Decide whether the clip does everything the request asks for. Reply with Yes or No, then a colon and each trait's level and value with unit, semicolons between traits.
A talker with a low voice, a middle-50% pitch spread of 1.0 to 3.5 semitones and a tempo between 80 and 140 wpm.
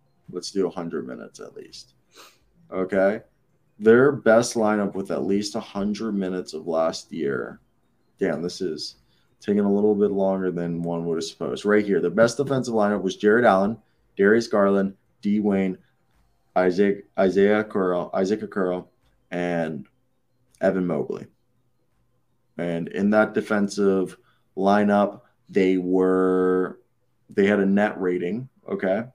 Yes: low, 100 Hz; narrow, 2.4 semitones; slow, 135 wpm